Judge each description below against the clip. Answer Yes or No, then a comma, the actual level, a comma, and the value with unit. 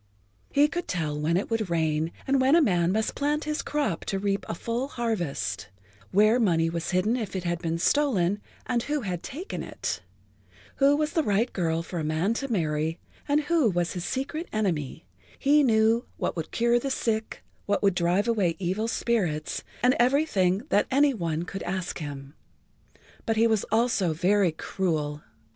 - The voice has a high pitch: Yes, high, 200 Hz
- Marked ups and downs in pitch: Yes, wide, 6.3 semitones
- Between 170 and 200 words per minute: Yes, average, 180 wpm